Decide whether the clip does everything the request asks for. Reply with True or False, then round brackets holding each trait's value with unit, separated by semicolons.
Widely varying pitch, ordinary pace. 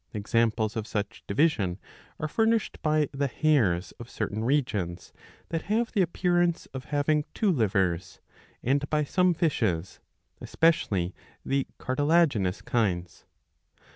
False (7.7 semitones; 125 wpm)